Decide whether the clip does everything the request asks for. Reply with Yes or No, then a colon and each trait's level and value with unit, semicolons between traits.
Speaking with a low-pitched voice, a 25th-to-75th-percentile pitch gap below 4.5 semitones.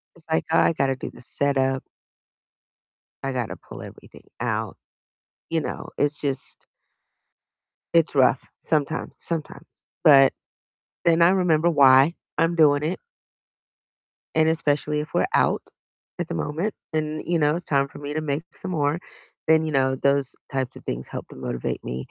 No: medium, 150 Hz; average, 2.9 semitones